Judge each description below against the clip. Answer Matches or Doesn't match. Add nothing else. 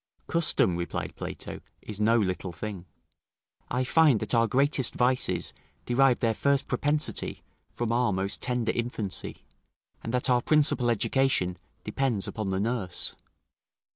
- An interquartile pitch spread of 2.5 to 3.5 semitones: Doesn't match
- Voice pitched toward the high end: Doesn't match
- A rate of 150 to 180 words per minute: Doesn't match